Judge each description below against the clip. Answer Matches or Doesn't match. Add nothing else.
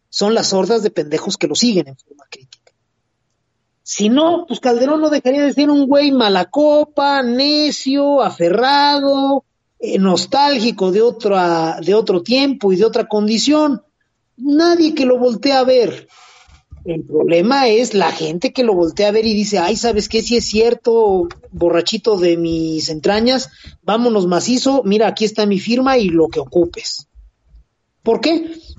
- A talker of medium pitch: Doesn't match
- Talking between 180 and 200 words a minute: Doesn't match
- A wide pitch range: Matches